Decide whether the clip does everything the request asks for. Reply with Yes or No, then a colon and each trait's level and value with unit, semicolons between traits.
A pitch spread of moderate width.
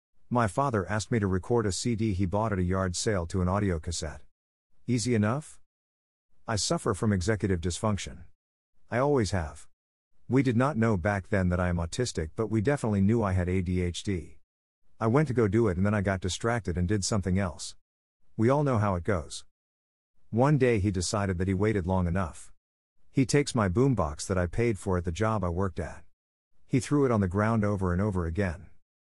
Yes: average, 4.4 semitones